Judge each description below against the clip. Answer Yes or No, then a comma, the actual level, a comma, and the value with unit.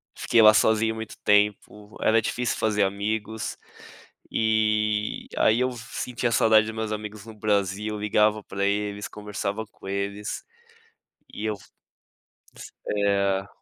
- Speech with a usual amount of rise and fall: No, narrow, 1.4 semitones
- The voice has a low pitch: Yes, low, 105 Hz